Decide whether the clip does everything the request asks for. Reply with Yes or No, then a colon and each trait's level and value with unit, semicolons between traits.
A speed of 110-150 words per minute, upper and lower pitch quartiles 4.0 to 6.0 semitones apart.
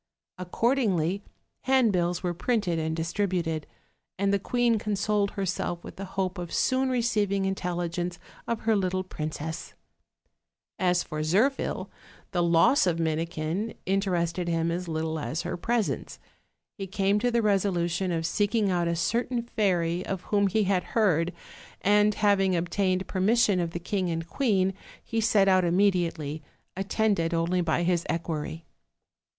No: average, 145 wpm; average, 3.3 semitones